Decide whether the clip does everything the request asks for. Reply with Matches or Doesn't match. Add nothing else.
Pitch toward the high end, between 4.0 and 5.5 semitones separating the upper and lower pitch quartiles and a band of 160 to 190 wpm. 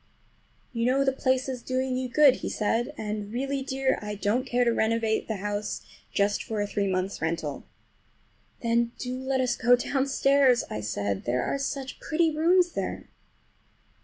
Matches